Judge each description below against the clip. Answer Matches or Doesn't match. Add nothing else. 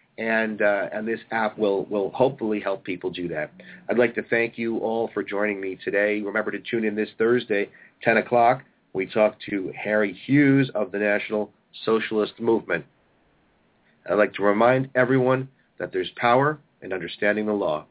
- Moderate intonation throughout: Doesn't match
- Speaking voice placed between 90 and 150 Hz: Matches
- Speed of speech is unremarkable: Matches